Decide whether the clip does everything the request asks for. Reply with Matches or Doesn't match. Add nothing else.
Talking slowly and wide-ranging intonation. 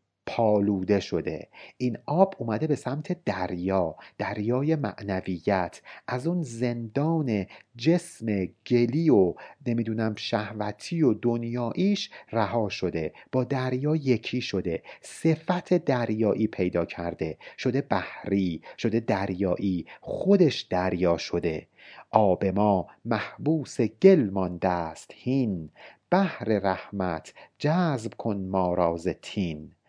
Matches